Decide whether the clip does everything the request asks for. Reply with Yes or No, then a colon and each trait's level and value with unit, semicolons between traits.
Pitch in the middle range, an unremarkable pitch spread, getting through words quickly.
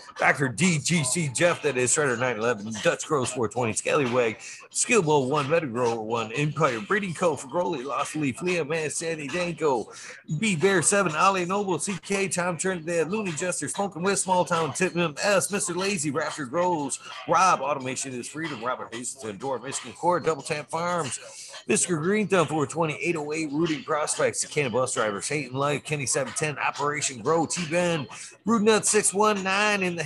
No: medium, 170 Hz; average, 3.8 semitones; average, 165 wpm